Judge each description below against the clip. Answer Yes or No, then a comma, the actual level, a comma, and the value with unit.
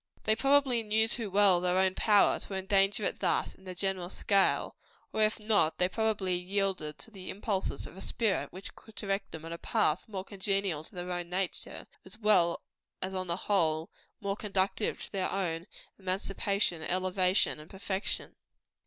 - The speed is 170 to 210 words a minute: Yes, average, 175 wpm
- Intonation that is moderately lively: No, narrow, 2.2 semitones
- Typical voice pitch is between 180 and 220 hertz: Yes, high, 190 Hz